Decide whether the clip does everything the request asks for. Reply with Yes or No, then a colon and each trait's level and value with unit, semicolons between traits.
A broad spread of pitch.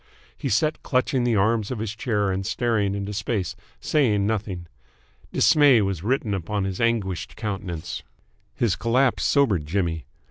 No: average, 3.4 semitones